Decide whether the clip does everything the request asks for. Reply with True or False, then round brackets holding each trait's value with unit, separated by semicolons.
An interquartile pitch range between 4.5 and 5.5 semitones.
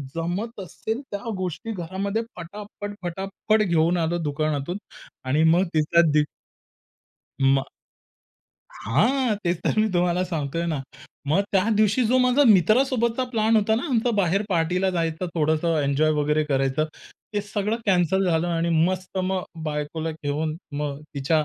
True (4.8 semitones)